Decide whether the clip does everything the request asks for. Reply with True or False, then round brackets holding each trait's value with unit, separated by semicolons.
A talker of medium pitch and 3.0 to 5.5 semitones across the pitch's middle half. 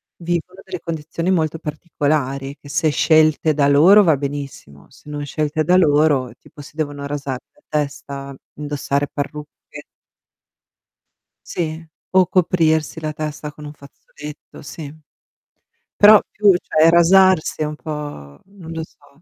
False (150 Hz; 2.5 semitones)